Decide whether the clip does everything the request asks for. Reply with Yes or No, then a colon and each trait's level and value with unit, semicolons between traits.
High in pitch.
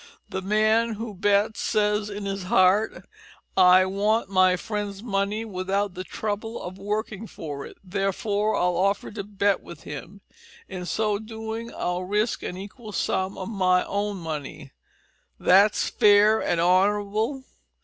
Yes: high, 200 Hz